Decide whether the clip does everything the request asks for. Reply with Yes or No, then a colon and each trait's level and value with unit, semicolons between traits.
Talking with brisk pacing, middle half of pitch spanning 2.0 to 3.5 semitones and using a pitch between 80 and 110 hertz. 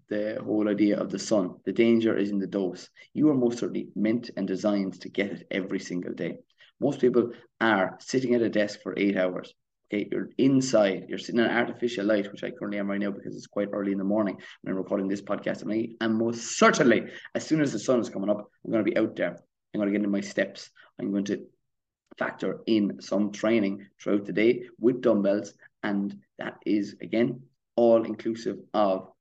Yes: fast, 215 wpm; narrow, 2.4 semitones; low, 105 Hz